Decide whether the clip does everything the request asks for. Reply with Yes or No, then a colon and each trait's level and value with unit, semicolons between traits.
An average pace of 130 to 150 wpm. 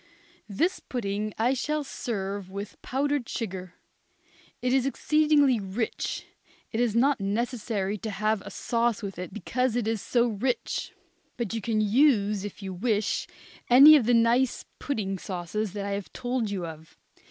No: average, 160 wpm